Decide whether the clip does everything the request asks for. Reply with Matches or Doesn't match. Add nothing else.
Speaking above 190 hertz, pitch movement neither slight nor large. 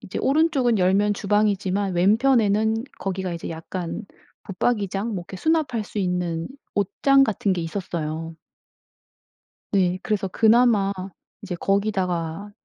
Matches